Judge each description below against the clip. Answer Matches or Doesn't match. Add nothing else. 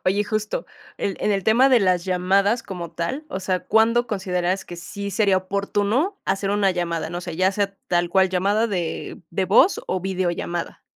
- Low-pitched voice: Doesn't match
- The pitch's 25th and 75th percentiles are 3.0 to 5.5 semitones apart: Doesn't match